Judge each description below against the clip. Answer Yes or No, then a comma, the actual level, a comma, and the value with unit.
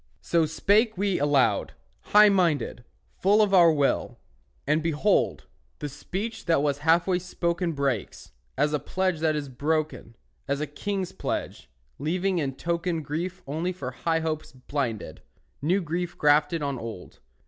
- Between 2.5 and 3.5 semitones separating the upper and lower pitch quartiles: No, average, 4.0 semitones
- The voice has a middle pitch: Yes, medium, 160 Hz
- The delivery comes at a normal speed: Yes, average, 150 wpm